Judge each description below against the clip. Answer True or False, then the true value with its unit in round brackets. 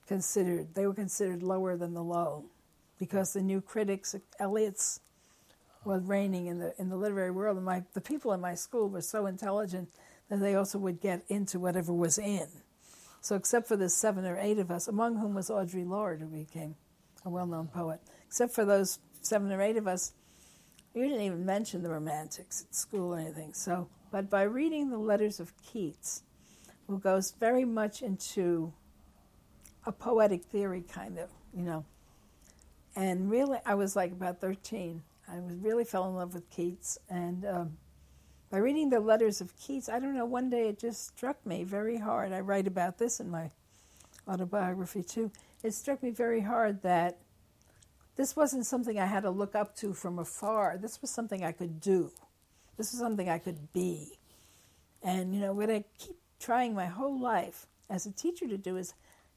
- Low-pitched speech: False (190 Hz)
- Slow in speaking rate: False (185 wpm)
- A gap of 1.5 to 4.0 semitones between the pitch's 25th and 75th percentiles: True (3.6 semitones)